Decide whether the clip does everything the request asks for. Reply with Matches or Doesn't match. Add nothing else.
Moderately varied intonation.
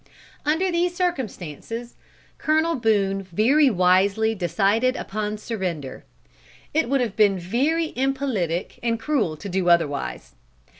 Doesn't match